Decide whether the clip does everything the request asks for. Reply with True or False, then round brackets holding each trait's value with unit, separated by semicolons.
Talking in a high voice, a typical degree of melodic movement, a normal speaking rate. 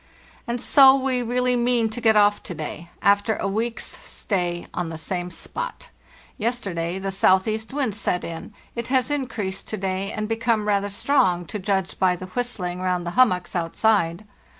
True (205 Hz; 4.7 semitones; 175 wpm)